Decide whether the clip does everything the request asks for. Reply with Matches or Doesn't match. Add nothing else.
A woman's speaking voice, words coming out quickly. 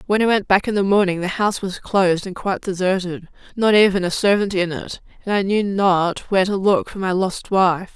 Matches